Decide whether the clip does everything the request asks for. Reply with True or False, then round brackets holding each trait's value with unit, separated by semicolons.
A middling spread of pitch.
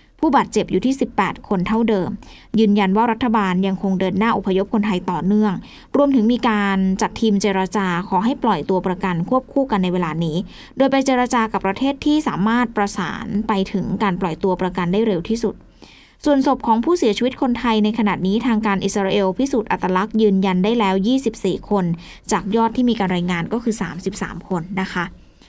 True (3.3 semitones)